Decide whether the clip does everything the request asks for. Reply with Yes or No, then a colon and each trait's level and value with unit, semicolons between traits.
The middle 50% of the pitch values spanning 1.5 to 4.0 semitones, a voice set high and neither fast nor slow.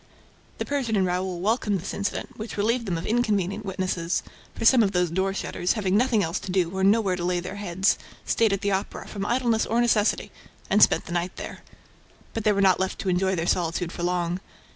No: average, 3.0 semitones; high, 195 Hz; fast, 220 wpm